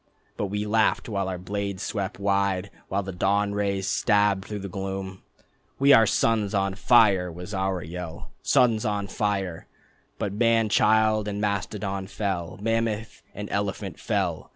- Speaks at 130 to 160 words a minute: Yes, average, 155 wpm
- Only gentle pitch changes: Yes, narrow, 1.6 semitones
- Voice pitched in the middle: No, low, 100 Hz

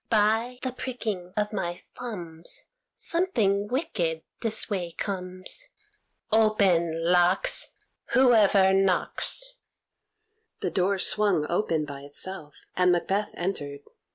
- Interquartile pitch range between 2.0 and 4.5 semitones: Yes, average, 3.9 semitones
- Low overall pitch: No, high, 195 Hz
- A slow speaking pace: Yes, slow, 100 wpm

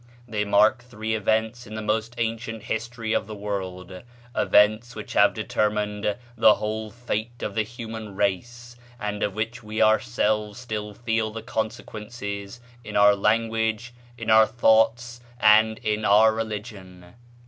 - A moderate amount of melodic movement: No, narrow, 1.5 semitones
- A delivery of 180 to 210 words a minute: No, average, 145 wpm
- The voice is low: Yes, low, 110 Hz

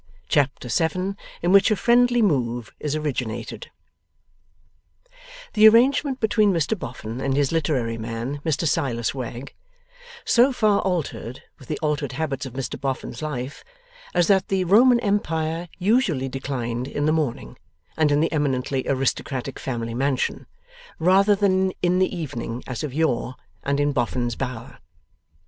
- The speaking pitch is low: No, medium, 145 Hz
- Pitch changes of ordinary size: No, wide, 6.6 semitones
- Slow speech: No, average, 145 wpm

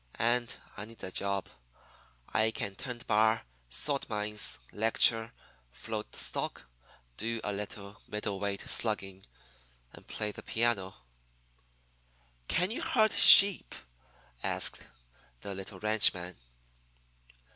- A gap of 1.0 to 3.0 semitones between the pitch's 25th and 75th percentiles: Yes, narrow, 2.5 semitones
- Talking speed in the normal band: No, slow, 110 wpm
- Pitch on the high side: No, low, 105 Hz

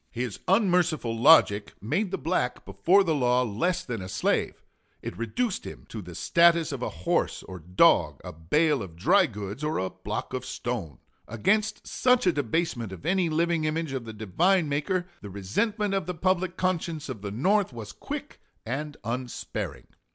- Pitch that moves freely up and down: Yes, wide, 8.8 semitones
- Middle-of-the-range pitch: Yes, medium, 145 Hz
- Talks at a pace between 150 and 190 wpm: Yes, average, 175 wpm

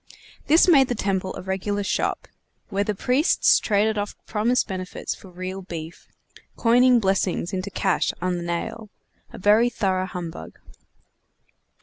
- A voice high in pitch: Yes, high, 195 Hz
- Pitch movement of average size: Yes, average, 3.2 semitones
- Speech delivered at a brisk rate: No, average, 140 wpm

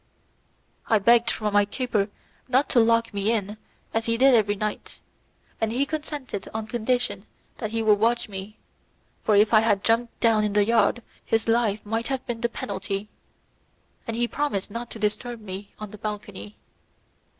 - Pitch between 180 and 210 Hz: No, high, 220 Hz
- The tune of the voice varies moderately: No, narrow, 2.3 semitones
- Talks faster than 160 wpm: Yes, average, 175 wpm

